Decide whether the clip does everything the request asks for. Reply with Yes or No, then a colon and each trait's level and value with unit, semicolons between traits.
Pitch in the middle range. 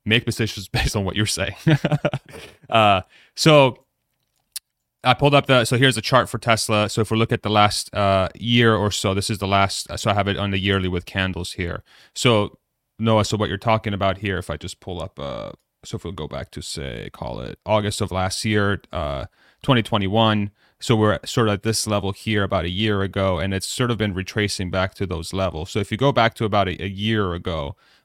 No: low, 105 Hz